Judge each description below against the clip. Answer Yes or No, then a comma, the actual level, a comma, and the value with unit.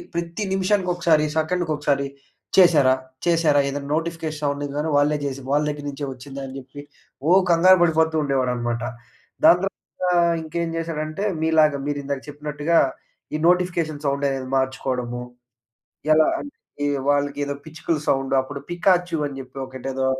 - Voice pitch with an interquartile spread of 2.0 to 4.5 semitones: Yes, average, 3.4 semitones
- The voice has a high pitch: No, medium, 150 Hz